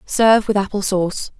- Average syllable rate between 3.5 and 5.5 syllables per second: No, 5.7 syllables/s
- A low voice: No, high, 200 Hz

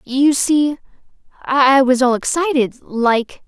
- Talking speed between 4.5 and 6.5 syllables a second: No, 3.8 syllables/s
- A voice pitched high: Yes, very high, 265 Hz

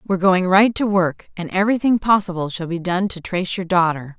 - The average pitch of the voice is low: No, medium, 185 Hz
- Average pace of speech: No, fast, 215 wpm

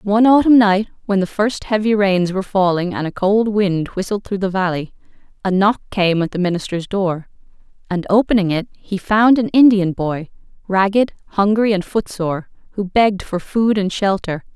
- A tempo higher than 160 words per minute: Yes, average, 180 wpm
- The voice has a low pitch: No, high, 195 Hz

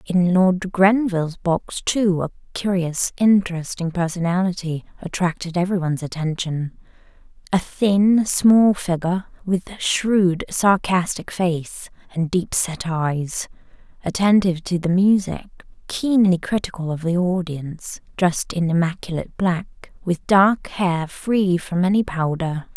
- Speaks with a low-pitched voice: No, medium, 180 Hz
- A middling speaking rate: No, slow, 115 wpm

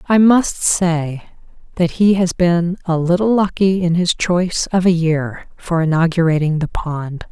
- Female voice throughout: Yes, female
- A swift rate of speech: No, average, 165 wpm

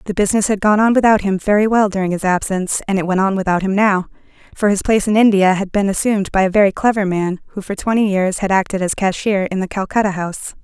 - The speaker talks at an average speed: No, fast, 250 wpm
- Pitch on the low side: No, high, 200 Hz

